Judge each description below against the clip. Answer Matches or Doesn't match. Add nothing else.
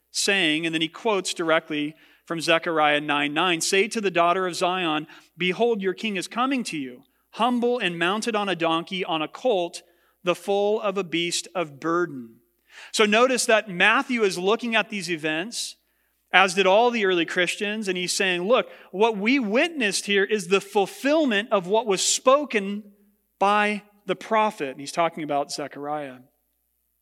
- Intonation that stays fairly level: Doesn't match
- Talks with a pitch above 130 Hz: Matches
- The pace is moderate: Matches